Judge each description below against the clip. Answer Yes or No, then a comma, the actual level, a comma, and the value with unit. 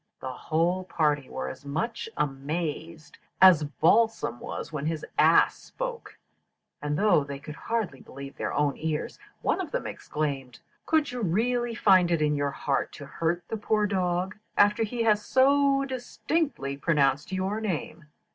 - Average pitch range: No, wide, 6.9 semitones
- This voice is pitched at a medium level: Yes, medium, 170 Hz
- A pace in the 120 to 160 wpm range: Yes, average, 155 wpm